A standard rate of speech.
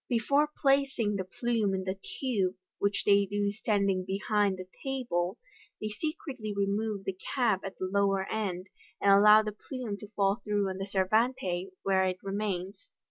Yes: average, 165 wpm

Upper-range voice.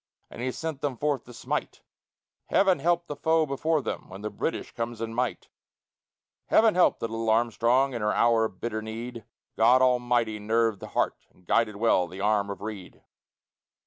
No: low, 115 Hz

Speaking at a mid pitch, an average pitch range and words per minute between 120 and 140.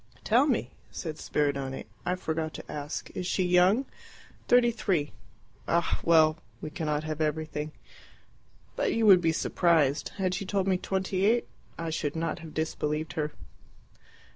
No: medium, 165 Hz; average, 3.7 semitones; average, 150 wpm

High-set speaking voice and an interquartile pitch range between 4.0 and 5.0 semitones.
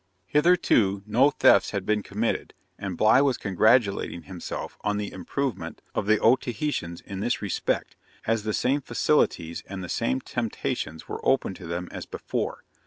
No: low, 105 Hz; average, 4.7 semitones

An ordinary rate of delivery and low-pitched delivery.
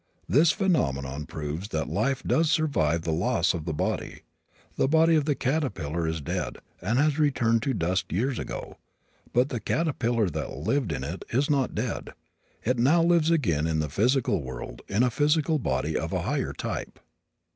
Yes: average, 180 wpm; low, 115 Hz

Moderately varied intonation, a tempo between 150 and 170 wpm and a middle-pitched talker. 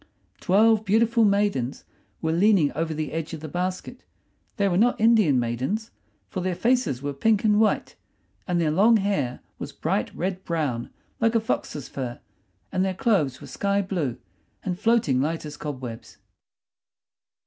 No: wide, 6.4 semitones; average, 160 wpm; medium, 180 Hz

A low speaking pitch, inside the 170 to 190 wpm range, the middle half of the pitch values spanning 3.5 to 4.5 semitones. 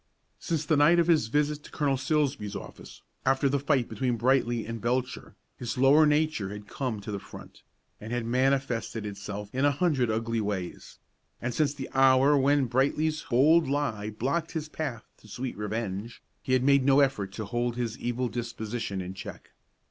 Yes: low, 130 Hz; average, 180 wpm; average, 4.1 semitones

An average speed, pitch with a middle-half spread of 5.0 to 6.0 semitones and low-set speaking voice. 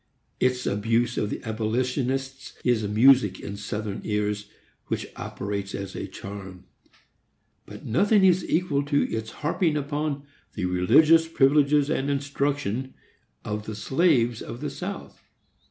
No: slow, 130 wpm; wide, 5.4 semitones; low, 125 Hz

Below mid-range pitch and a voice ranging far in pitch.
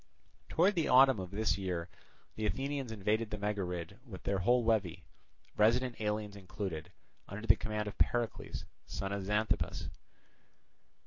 No: low, 105 Hz; average, 2.9 semitones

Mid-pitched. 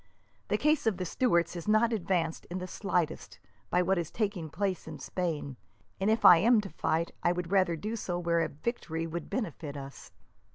Yes: medium, 175 Hz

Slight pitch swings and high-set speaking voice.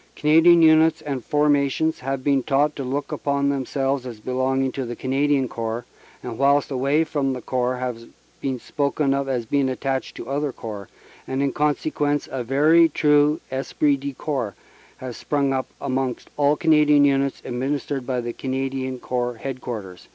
No: narrow, 2.2 semitones; low, 135 Hz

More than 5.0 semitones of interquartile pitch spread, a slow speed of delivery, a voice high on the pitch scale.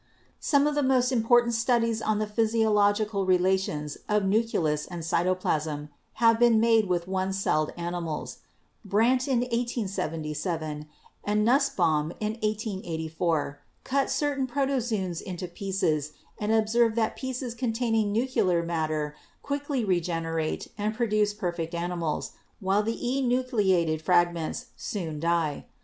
Yes: wide, 5.5 semitones; slow, 120 wpm; high, 205 Hz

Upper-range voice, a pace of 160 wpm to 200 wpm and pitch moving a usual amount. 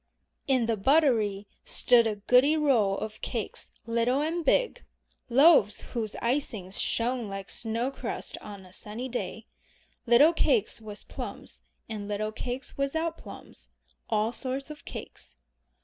No: high, 235 Hz; slow, 135 wpm; average, 4.5 semitones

